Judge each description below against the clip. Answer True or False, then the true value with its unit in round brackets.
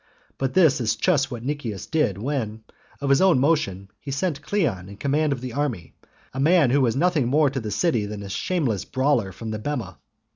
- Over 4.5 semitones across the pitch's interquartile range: True (5.4 semitones)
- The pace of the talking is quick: True (210 wpm)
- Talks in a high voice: False (135 Hz)